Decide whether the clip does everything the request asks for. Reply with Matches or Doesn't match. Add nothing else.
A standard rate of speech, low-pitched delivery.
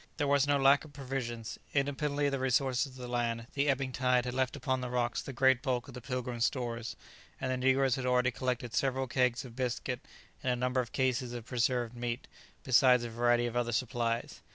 Doesn't match